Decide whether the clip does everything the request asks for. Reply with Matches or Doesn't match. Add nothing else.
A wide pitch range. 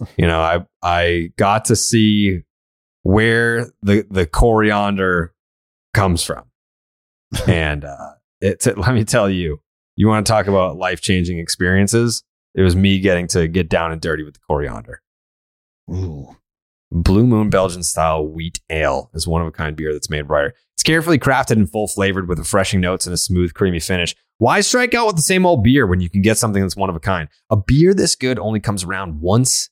Doesn't match